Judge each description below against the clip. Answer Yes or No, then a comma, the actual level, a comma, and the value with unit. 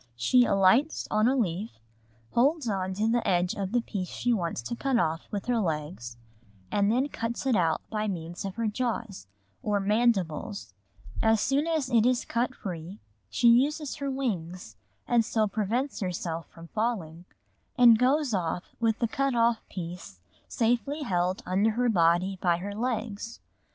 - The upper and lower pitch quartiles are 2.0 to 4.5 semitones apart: No, average, 5.0 semitones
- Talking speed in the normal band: Yes, average, 170 wpm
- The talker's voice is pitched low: No, high, 215 Hz